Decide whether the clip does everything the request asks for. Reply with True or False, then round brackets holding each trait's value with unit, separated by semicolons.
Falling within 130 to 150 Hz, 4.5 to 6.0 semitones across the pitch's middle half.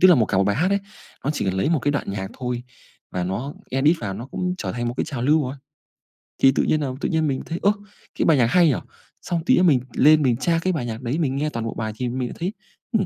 True (135 Hz; 5.2 semitones)